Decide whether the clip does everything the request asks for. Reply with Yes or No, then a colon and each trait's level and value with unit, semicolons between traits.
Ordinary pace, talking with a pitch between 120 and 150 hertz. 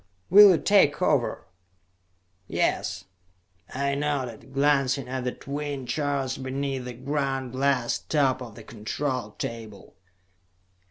No: slow, 115 wpm; low, 135 Hz